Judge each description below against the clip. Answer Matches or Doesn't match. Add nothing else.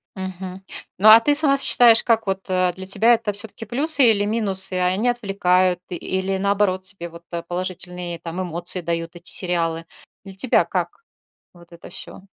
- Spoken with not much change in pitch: Doesn't match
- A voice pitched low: Doesn't match